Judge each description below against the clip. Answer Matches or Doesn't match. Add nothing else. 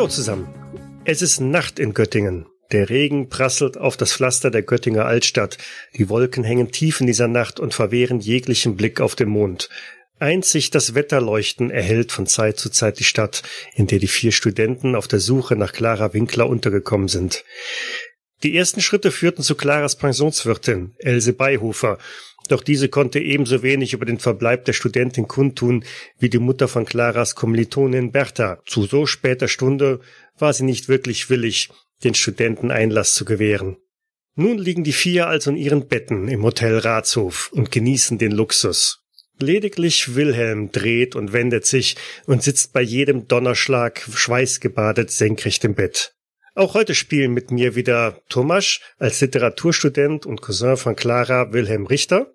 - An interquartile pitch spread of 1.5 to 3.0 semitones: Doesn't match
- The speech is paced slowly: Doesn't match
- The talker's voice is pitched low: Matches